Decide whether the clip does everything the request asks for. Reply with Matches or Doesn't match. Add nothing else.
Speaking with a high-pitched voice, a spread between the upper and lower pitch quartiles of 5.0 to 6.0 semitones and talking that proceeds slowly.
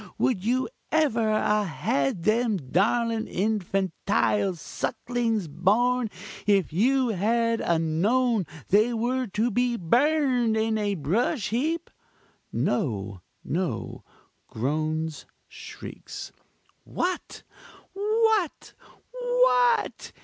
Matches